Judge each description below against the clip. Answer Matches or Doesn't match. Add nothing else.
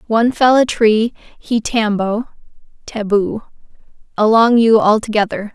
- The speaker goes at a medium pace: Doesn't match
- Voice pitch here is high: Matches